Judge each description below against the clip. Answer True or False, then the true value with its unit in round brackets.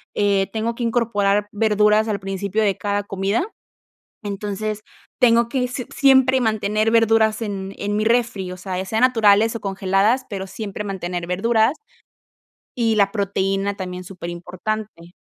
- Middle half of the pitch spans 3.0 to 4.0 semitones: False (2.5 semitones)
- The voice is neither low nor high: False (205 Hz)